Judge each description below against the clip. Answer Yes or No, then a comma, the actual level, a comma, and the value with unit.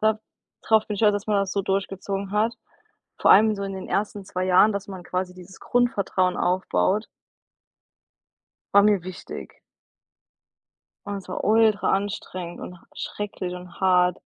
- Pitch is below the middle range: No, high, 195 Hz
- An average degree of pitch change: No, narrow, 2.1 semitones